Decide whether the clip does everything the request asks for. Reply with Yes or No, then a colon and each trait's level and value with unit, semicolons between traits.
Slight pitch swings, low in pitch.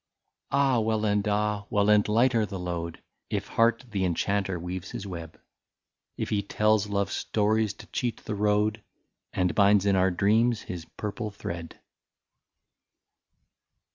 Yes: narrow, 2.1 semitones; low, 105 Hz